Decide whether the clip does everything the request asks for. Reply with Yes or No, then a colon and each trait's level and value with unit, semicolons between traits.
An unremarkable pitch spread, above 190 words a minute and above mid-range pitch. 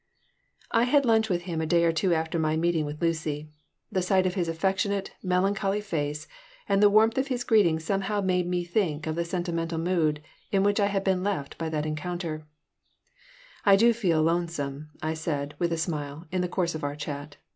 No: average, 3.7 semitones; average, 200 wpm; medium, 175 Hz